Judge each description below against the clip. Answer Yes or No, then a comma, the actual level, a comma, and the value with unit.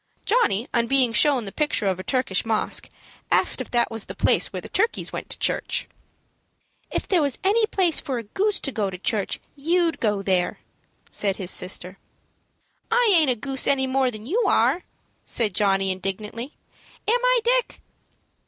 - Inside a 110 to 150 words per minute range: No, average, 180 wpm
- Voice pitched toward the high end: Yes, very high, 250 Hz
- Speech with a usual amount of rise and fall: No, wide, 8.9 semitones